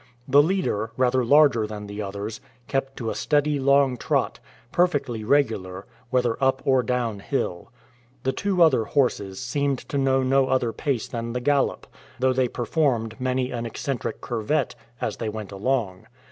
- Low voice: Yes, low, 130 Hz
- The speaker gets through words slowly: No, average, 160 wpm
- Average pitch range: Yes, average, 3.6 semitones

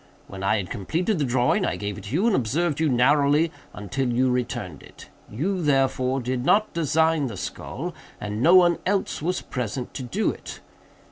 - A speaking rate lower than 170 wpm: No, average, 190 wpm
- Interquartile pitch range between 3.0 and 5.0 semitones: No, wide, 5.4 semitones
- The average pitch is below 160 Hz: Yes, low, 135 Hz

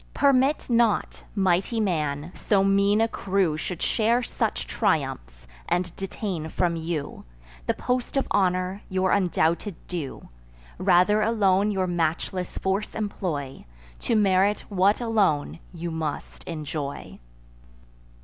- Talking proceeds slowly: Yes, slow, 120 wpm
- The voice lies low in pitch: No, medium, 185 Hz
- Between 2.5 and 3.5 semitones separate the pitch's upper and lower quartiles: No, average, 4.0 semitones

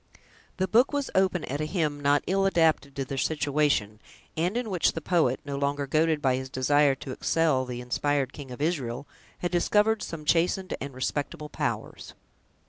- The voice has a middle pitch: Yes, medium, 150 Hz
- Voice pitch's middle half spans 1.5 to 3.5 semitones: No, average, 4.2 semitones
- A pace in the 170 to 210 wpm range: Yes, average, 180 wpm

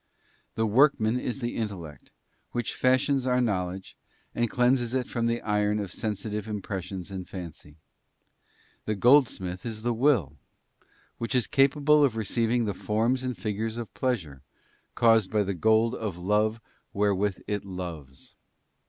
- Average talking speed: Yes, average, 160 wpm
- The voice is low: Yes, low, 110 Hz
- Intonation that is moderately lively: Yes, average, 3.8 semitones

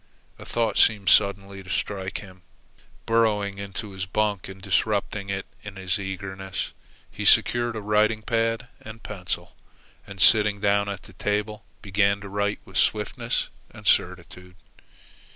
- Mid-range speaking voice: No, low, 100 Hz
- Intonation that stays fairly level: Yes, narrow, 1.8 semitones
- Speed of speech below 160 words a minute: Yes, average, 145 wpm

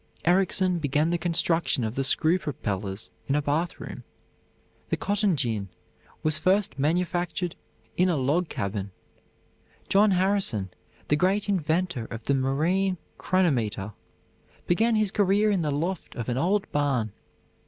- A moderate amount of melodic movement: No, wide, 5.8 semitones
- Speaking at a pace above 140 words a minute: No, slow, 135 wpm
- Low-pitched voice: No, medium, 165 Hz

